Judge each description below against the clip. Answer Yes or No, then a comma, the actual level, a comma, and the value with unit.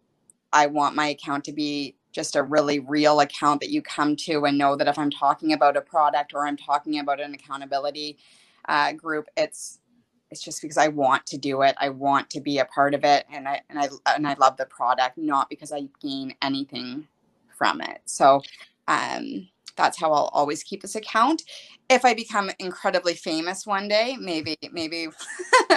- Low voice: No, medium, 145 Hz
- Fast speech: No, average, 195 wpm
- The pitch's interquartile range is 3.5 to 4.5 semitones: No, average, 2.8 semitones